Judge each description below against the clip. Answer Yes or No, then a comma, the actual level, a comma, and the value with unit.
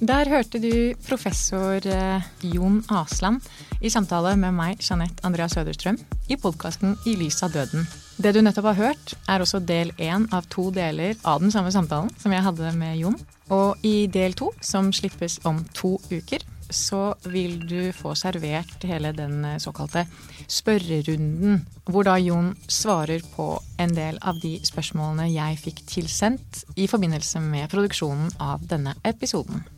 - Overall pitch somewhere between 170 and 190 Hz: Yes, medium, 185 Hz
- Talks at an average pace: Yes, average, 155 wpm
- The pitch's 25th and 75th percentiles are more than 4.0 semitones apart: No, average, 3.7 semitones